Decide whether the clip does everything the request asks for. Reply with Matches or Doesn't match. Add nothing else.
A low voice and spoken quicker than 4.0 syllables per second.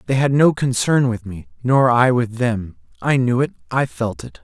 Matches